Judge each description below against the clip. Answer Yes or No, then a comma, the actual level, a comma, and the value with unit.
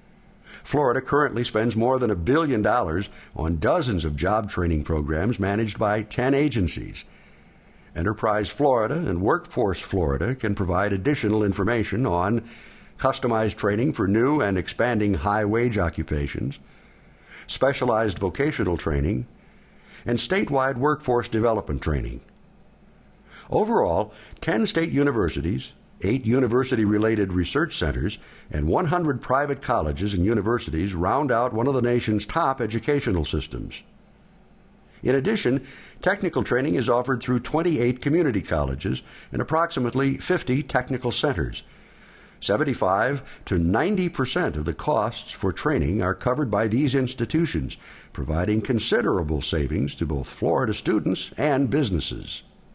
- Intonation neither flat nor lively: No, wide, 6.0 semitones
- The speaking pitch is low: Yes, low, 110 Hz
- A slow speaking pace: Yes, slow, 120 wpm